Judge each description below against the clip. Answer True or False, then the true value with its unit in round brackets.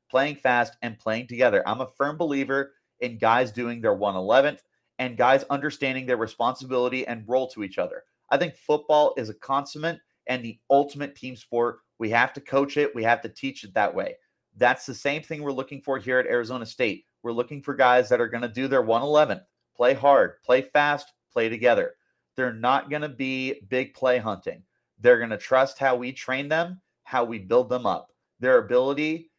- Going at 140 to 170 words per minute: False (195 wpm)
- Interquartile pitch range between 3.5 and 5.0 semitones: False (2.9 semitones)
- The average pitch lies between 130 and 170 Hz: True (135 Hz)